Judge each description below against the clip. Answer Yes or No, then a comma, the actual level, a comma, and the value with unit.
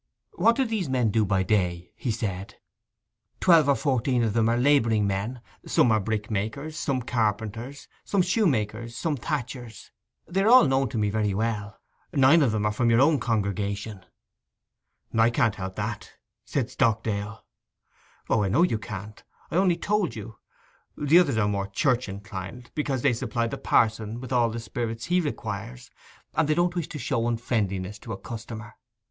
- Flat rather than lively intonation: No, average, 4.5 semitones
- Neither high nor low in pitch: No, low, 115 Hz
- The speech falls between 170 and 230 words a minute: Yes, average, 175 wpm